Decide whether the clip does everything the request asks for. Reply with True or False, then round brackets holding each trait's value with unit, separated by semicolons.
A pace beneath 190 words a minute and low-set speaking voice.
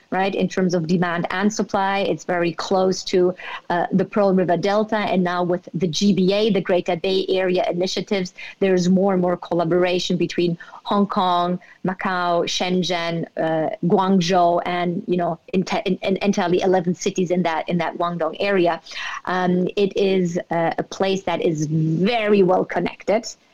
False (170 wpm; 185 Hz)